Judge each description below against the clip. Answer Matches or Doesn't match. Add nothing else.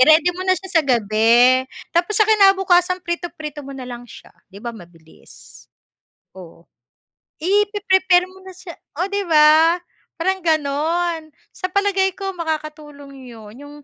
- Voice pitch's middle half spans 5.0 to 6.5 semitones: Matches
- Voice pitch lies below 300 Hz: Doesn't match